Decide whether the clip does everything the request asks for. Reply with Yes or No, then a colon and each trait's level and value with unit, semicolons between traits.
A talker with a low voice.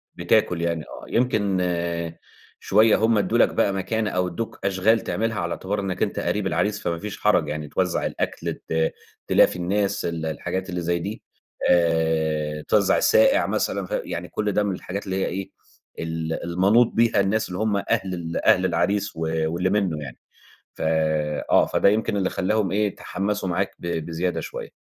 Yes: very low, 95 Hz